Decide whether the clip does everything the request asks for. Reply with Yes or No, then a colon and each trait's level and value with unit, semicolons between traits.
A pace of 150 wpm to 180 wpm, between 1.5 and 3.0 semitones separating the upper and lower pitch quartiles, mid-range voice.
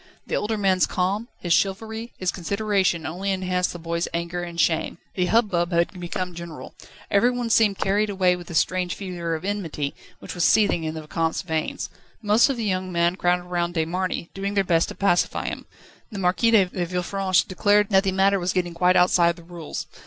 No: average, 195 wpm; narrow, 2.5 semitones; medium, 180 Hz